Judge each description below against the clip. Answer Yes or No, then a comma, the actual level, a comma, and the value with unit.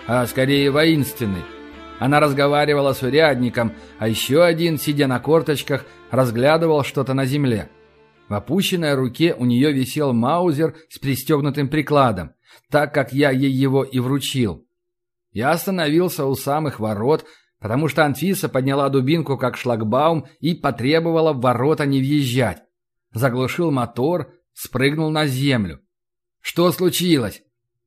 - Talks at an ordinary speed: Yes, average, 125 wpm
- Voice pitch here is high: No, low, 135 Hz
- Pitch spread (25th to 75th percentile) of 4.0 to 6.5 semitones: Yes, average, 4.4 semitones